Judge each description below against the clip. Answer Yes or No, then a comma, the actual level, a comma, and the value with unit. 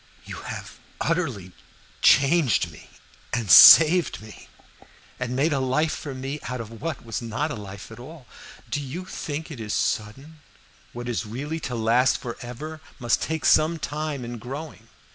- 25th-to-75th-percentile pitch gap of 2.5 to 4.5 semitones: No, average, 5.0 semitones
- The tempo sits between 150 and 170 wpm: Yes, average, 160 wpm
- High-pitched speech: No, low, 130 Hz